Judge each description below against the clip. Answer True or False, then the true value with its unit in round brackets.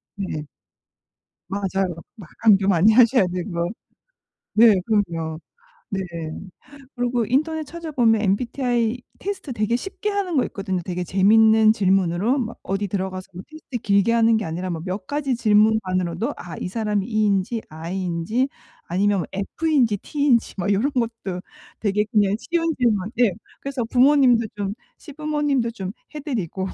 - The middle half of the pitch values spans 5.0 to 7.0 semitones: False (4.6 semitones)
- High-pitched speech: True (215 Hz)